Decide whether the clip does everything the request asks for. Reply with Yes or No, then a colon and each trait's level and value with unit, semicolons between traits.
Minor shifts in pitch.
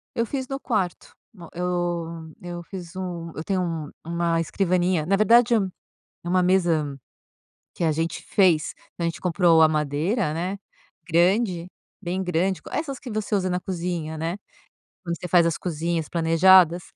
Yes: narrow, 2.3 semitones